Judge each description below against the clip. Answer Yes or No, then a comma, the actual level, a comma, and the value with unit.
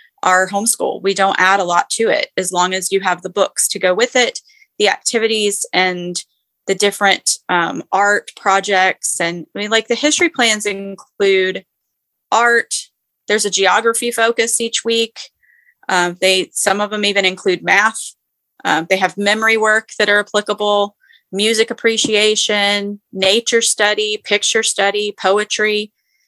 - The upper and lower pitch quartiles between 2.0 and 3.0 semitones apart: Yes, average, 2.7 semitones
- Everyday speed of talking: Yes, average, 150 wpm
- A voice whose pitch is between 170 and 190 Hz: No, high, 205 Hz